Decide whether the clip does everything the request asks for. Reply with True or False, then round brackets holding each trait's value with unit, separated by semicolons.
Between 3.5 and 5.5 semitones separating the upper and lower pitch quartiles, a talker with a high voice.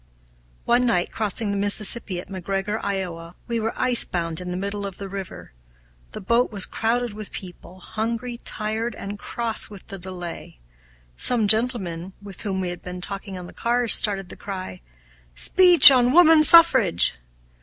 True (4.1 semitones; 200 Hz)